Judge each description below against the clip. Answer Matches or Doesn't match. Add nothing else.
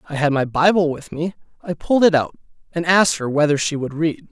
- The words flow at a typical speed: Doesn't match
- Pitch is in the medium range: Matches